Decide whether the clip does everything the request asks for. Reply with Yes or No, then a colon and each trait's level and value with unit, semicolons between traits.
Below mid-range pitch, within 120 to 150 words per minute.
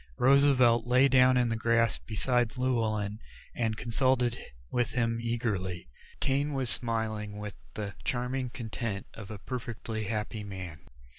Yes: low, 115 Hz; slow, 135 wpm